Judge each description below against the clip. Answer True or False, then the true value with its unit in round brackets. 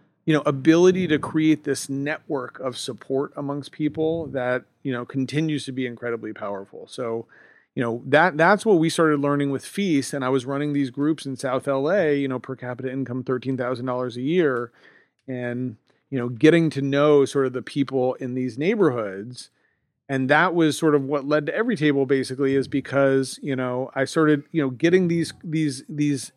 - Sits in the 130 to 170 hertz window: True (140 Hz)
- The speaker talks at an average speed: True (195 wpm)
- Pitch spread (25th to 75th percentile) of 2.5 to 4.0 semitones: True (2.8 semitones)